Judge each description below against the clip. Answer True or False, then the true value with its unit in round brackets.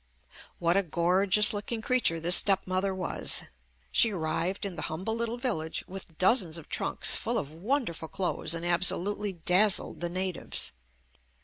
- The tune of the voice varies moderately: True (3.4 semitones)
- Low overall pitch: False (185 Hz)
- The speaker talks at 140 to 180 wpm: True (150 wpm)